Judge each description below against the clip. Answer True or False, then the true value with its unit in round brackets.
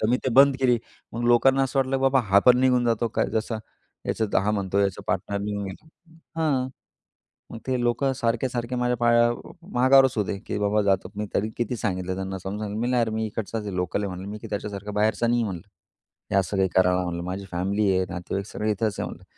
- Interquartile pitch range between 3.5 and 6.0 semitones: True (3.9 semitones)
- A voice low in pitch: True (110 Hz)